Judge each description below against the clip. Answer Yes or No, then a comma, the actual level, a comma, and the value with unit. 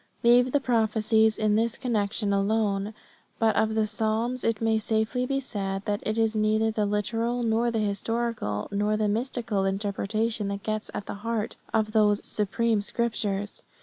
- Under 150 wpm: No, average, 165 wpm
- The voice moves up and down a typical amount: No, narrow, 1.8 semitones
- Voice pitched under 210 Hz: No, high, 220 Hz